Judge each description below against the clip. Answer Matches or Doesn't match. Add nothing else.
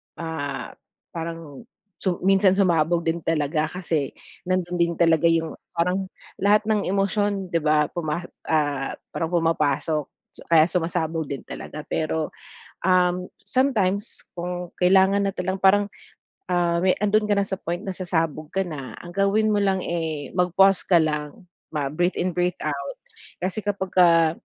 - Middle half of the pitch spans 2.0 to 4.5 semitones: Matches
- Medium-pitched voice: Matches